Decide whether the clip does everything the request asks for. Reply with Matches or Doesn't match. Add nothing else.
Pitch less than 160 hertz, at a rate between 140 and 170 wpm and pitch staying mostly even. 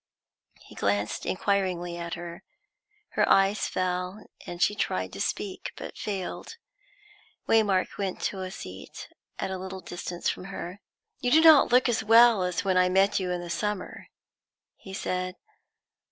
Doesn't match